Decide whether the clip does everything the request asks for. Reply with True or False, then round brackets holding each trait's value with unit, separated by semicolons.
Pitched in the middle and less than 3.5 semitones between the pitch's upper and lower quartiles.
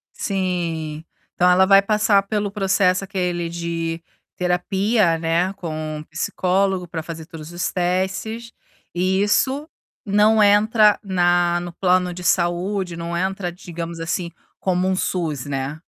True (180 Hz; 2.6 semitones)